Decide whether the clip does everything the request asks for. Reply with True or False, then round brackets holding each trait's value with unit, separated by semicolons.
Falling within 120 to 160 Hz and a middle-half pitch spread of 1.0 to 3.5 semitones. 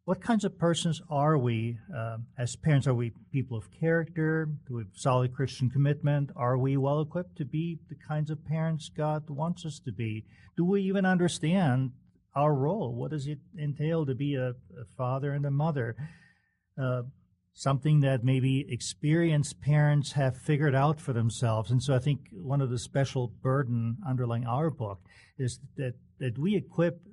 False (140 Hz; 3.9 semitones)